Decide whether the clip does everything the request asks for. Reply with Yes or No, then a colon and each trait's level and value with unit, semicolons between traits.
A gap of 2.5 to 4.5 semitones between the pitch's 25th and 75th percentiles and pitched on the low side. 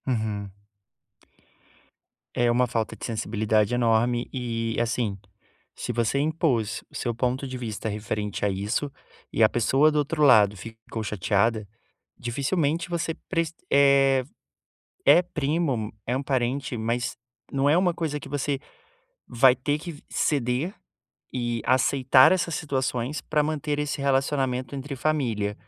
Yes: average, 4.2 semitones; low, 125 Hz